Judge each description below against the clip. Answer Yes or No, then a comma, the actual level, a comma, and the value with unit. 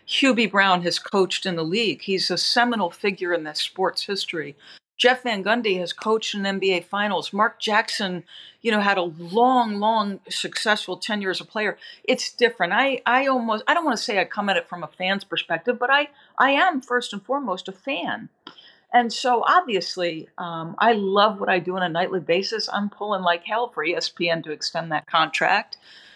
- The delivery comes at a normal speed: Yes, average, 195 wpm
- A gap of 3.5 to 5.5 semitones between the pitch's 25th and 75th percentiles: Yes, average, 4.6 semitones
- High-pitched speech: Yes, high, 200 Hz